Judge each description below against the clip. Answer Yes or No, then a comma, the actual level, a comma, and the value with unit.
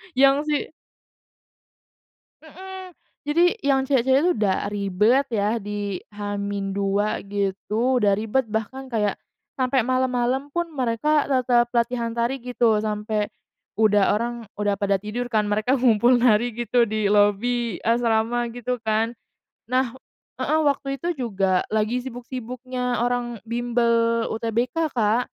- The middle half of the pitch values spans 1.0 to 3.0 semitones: No, average, 3.4 semitones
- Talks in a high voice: Yes, high, 235 Hz